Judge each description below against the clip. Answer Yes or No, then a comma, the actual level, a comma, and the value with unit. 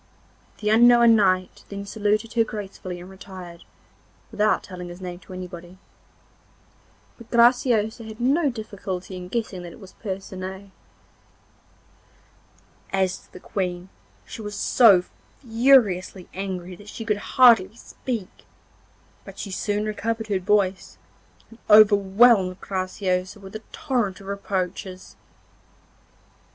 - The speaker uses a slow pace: Yes, slow, 120 wpm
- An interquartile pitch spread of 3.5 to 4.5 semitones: No, average, 3.1 semitones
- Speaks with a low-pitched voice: No, high, 200 Hz